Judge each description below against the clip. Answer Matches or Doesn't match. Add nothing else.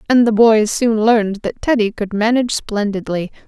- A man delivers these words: Doesn't match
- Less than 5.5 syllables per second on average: Matches